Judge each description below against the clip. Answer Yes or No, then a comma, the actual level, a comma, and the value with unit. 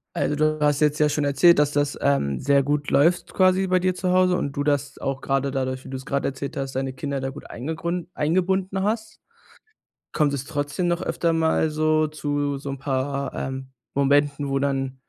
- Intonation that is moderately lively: Yes, average, 3.0 semitones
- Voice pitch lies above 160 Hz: No, medium, 145 Hz